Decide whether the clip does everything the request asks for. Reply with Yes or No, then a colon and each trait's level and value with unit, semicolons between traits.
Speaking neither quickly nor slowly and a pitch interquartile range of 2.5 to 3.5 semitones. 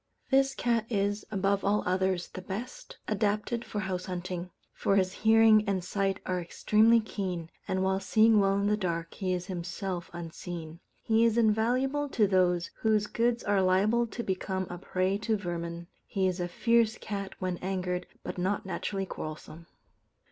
Yes: average, 170 wpm; average, 3.1 semitones